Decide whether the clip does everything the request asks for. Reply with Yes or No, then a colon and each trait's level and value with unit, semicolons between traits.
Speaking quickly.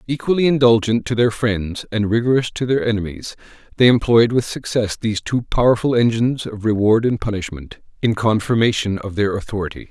No: average, 165 wpm